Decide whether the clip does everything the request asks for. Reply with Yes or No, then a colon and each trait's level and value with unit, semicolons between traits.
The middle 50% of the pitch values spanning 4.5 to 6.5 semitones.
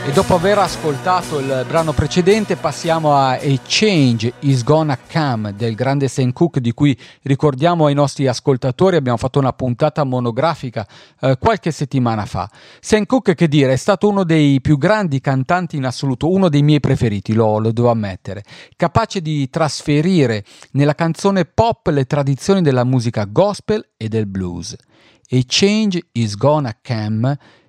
Yes: average, 5.1 semitones